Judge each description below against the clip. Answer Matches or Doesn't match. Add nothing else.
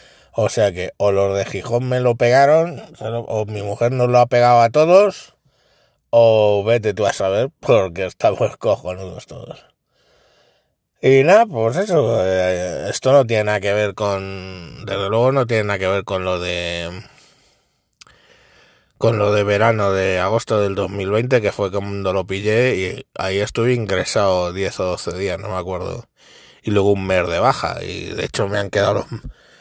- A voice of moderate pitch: Doesn't match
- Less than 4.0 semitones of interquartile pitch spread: Matches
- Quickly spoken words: Doesn't match